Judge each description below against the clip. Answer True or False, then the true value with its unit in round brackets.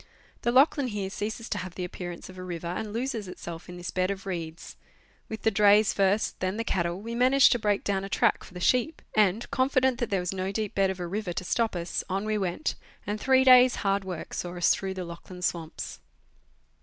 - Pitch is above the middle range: True (195 Hz)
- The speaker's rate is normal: False (230 wpm)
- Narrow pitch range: False (3.8 semitones)